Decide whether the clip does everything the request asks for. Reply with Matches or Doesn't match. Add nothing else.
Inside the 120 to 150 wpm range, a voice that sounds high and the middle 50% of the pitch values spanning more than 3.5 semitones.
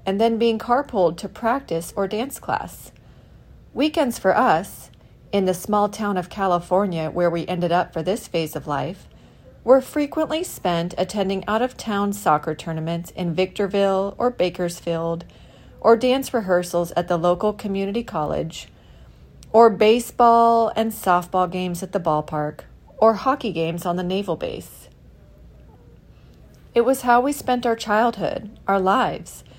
Matches